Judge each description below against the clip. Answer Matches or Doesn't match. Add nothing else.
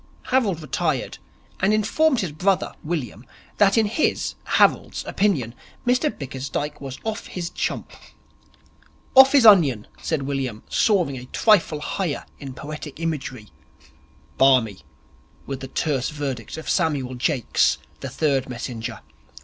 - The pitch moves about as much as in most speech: Doesn't match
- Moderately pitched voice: Matches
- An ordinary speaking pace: Doesn't match